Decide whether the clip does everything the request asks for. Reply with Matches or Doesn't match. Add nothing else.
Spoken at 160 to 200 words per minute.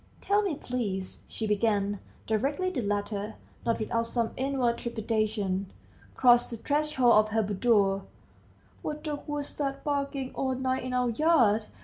Doesn't match